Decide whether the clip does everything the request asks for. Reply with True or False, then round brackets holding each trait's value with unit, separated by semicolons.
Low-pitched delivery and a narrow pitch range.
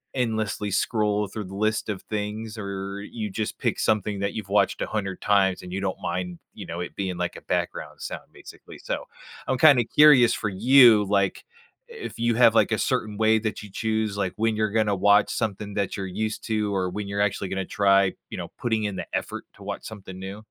True (105 Hz; 2.0 semitones)